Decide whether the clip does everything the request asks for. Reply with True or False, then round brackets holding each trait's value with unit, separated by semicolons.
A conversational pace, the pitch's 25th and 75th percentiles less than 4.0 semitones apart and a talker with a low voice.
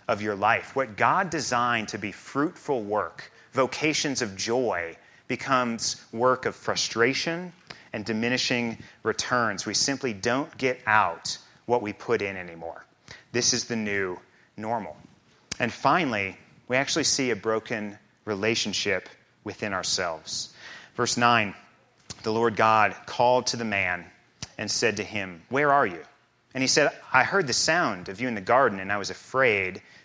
True (155 wpm; 3.3 semitones; 115 Hz)